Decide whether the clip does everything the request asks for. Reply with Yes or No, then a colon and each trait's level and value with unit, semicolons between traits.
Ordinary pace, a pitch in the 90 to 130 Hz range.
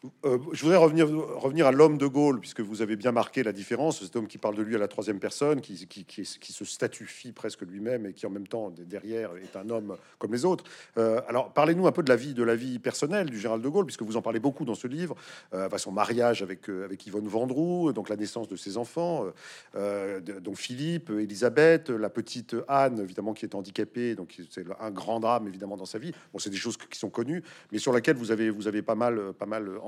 No: fast, 245 wpm; low, 115 Hz